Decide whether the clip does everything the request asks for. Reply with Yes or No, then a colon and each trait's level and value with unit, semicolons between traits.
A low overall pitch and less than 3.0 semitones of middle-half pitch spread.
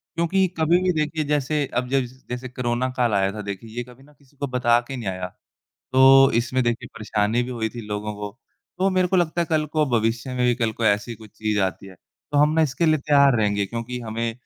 No: low, 125 Hz; average, 4.6 semitones